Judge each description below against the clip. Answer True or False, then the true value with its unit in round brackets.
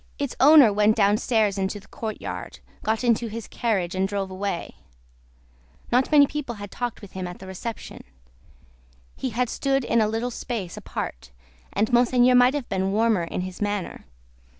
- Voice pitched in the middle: False (220 Hz)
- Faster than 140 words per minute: True (170 wpm)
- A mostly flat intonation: False (4.0 semitones)